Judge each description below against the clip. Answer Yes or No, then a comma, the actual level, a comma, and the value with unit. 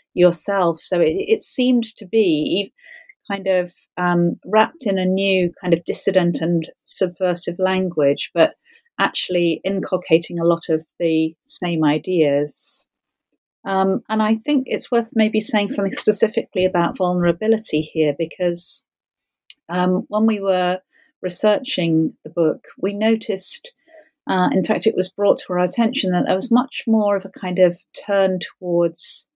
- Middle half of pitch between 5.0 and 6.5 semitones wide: No, average, 4.1 semitones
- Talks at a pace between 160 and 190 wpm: No, average, 145 wpm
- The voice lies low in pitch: No, high, 190 Hz